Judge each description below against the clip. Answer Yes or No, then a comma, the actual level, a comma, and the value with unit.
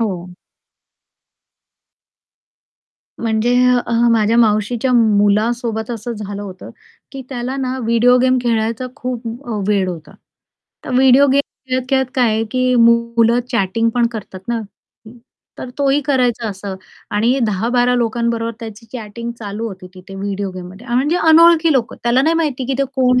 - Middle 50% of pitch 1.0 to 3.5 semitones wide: Yes, average, 3.1 semitones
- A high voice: Yes, high, 235 Hz